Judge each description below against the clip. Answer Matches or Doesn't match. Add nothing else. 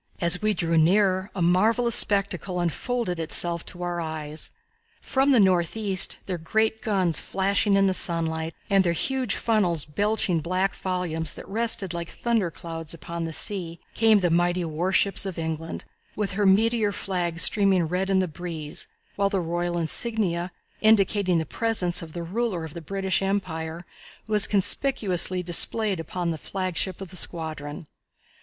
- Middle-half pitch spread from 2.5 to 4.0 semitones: Matches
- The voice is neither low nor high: Matches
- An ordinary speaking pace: Matches